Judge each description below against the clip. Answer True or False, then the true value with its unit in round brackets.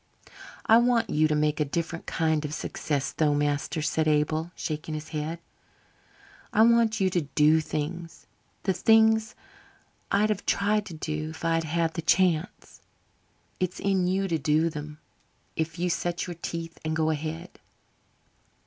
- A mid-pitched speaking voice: True (165 Hz)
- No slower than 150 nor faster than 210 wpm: True (160 wpm)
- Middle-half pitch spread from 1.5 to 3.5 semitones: True (3.1 semitones)